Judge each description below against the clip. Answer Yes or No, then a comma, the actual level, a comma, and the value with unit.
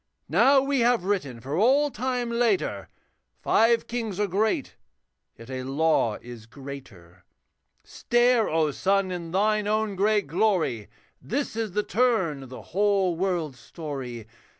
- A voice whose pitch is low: No, high, 195 Hz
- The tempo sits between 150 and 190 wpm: No, average, 140 wpm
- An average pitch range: No, wide, 8.2 semitones